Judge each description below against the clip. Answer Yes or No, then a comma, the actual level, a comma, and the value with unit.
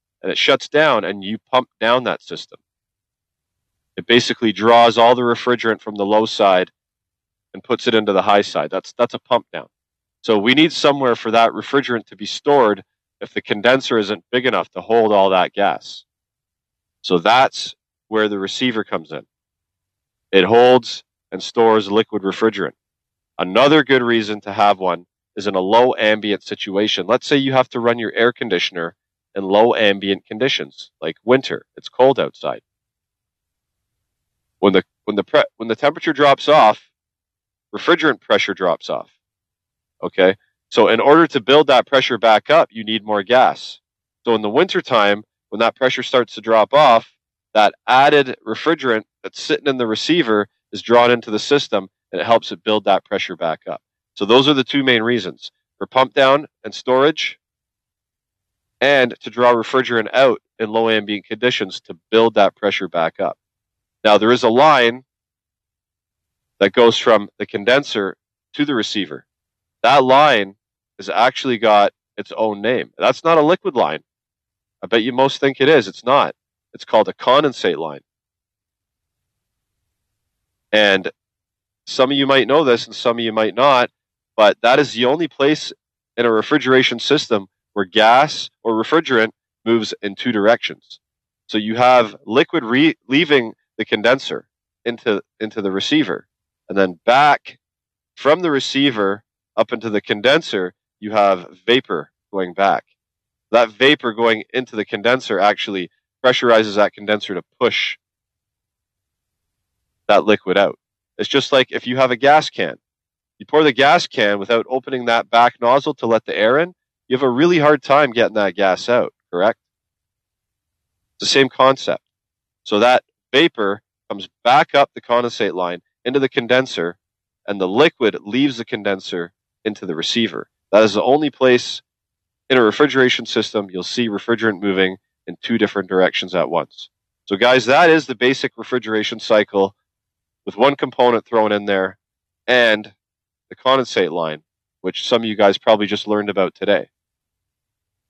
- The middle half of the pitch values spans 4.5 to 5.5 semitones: No, average, 3.7 semitones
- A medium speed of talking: Yes, average, 165 wpm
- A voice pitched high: No, low, 110 Hz